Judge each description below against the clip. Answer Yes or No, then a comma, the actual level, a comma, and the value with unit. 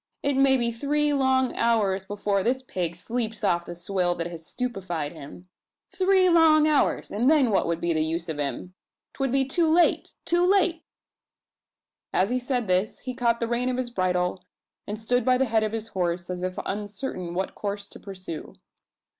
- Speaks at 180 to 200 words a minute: Yes, average, 190 wpm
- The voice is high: Yes, high, 220 Hz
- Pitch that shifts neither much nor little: No, wide, 6.3 semitones